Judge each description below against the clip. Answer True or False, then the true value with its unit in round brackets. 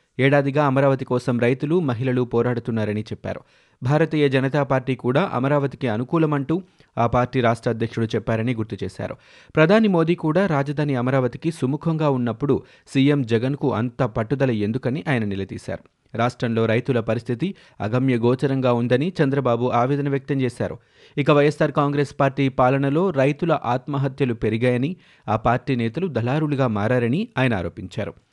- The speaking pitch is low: True (130 Hz)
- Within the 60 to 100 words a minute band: False (125 wpm)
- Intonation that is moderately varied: True (3.4 semitones)